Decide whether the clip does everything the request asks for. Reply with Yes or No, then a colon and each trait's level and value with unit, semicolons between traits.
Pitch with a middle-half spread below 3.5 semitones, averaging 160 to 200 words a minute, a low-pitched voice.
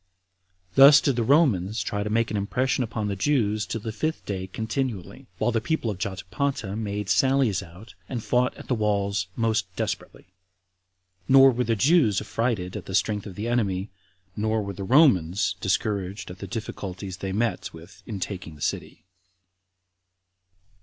No: average, 3.8 semitones; average, 165 wpm; low, 105 Hz